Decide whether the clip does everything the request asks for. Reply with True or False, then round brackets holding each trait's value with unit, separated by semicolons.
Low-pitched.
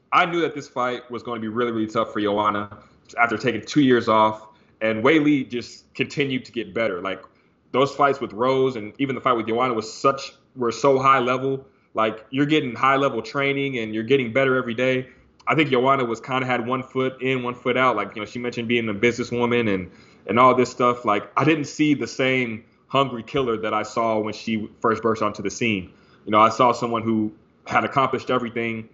True (120 Hz)